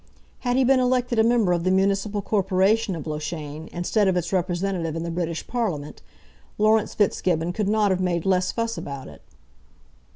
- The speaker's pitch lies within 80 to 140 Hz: No, high, 190 Hz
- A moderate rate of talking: Yes, average, 175 wpm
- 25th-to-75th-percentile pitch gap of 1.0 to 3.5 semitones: No, average, 4.1 semitones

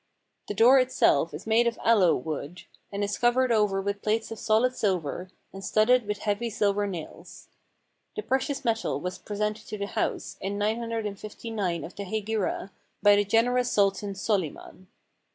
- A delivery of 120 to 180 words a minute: Yes, average, 170 wpm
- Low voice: No, high, 210 Hz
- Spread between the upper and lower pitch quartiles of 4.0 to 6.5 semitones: No, average, 2.7 semitones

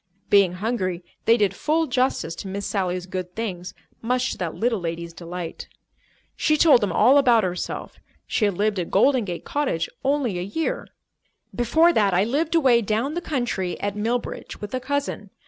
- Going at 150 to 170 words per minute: No, average, 180 wpm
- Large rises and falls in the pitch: Yes, wide, 6.0 semitones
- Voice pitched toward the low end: No, high, 215 Hz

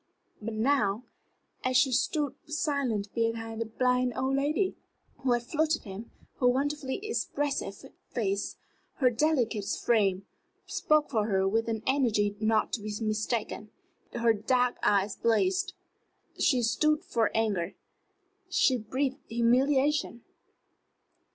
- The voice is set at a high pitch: Yes, high, 240 Hz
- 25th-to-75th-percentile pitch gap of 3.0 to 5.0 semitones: Yes, average, 4.3 semitones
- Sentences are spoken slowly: Yes, slow, 120 wpm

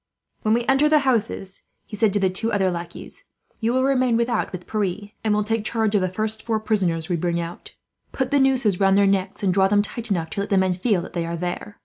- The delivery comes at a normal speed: No, fast, 255 wpm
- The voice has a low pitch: No, high, 205 Hz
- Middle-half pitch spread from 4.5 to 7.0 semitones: No, average, 3.6 semitones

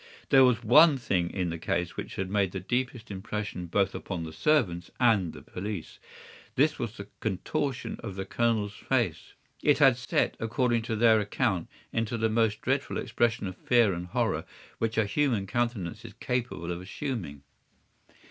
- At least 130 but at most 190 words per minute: Yes, average, 170 wpm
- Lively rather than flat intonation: No, average, 4.3 semitones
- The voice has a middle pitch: No, low, 110 Hz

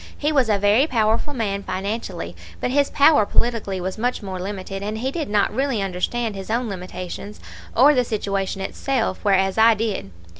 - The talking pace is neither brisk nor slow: Yes, average, 180 wpm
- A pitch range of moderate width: Yes, average, 3.9 semitones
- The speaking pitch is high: Yes, high, 210 Hz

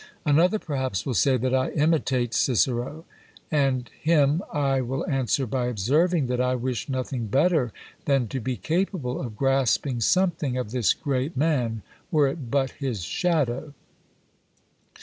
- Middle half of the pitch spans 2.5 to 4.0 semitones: Yes, average, 3.2 semitones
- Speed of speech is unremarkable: Yes, average, 145 wpm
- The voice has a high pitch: No, low, 135 Hz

